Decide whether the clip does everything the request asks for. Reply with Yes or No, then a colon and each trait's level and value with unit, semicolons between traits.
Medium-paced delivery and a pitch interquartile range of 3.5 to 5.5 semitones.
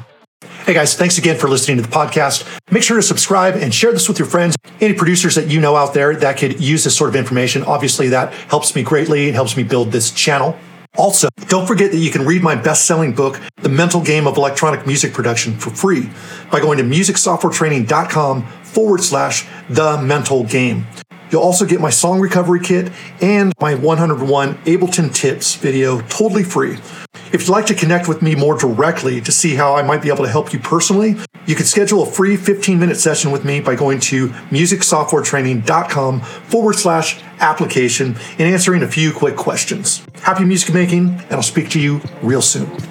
Yes: average, 195 wpm; average, 4.3 semitones